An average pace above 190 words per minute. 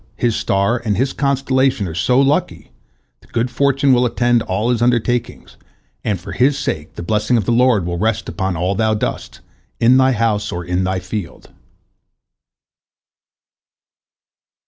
No: average, 155 wpm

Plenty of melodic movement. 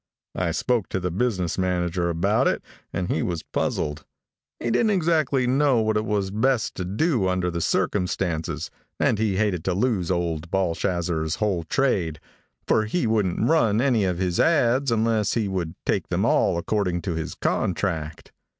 No: average, 4.9 semitones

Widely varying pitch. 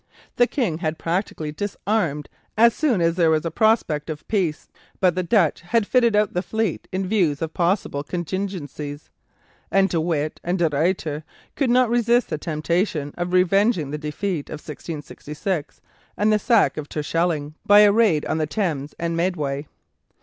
No: average, 5.0 semitones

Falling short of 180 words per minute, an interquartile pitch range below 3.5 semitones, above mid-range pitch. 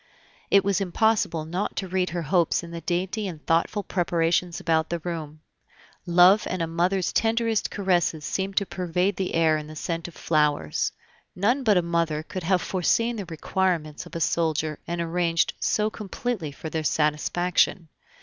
No: average, 170 wpm; average, 2.9 semitones; medium, 175 Hz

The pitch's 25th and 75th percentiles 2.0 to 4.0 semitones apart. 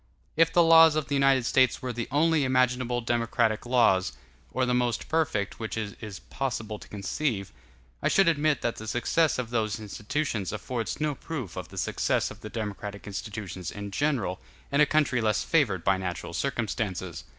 No: average, 5.2 semitones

